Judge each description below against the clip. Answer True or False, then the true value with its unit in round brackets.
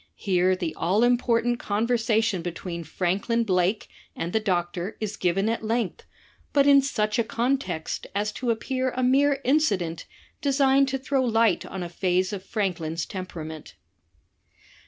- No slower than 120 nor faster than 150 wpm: True (145 wpm)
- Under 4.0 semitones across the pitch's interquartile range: False (5.3 semitones)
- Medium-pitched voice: False (215 Hz)